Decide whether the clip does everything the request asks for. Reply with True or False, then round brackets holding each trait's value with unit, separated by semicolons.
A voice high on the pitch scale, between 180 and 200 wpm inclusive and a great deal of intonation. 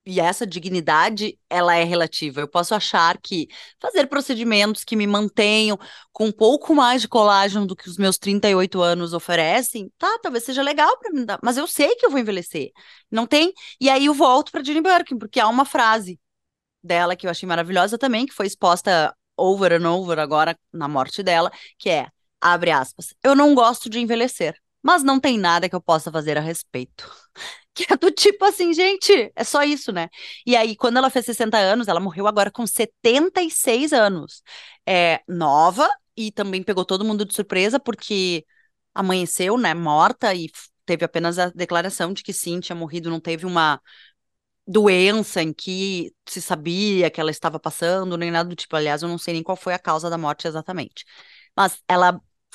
True (195 Hz; 185 wpm; 5.8 semitones)